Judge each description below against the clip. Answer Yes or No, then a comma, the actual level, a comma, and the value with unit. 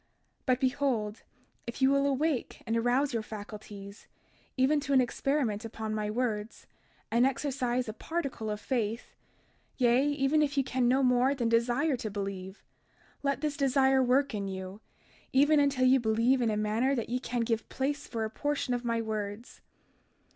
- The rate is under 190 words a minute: Yes, average, 175 wpm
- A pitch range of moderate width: Yes, average, 3.8 semitones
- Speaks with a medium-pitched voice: No, high, 245 Hz